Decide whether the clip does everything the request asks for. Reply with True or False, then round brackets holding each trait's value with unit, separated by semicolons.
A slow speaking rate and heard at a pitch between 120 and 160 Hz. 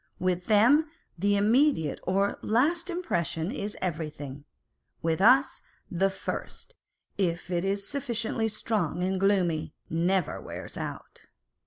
False (120 wpm; 195 Hz)